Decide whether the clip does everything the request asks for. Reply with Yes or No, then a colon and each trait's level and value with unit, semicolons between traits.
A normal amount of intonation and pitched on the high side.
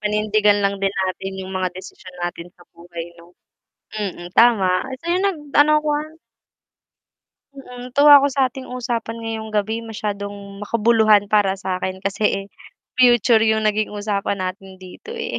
Yes: average, 3.8 semitones; high, 210 Hz